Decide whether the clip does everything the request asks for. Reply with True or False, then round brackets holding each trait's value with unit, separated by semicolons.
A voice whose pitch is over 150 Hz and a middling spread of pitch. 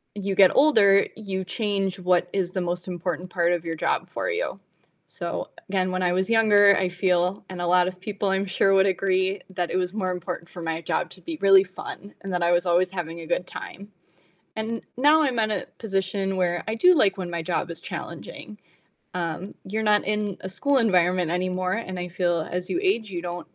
False (185 Hz; 2.3 semitones)